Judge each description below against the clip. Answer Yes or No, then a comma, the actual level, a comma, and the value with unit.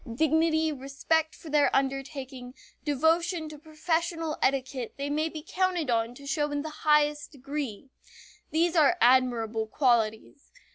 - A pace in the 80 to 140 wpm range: Yes, slow, 135 wpm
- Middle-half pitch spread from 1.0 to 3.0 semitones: No, average, 3.4 semitones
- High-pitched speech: Yes, very high, 290 Hz